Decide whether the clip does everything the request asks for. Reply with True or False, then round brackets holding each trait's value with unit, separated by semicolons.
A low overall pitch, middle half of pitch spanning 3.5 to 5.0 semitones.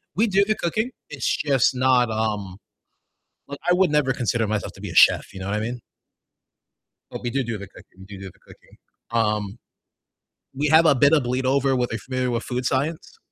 True (125 Hz; 4.6 semitones)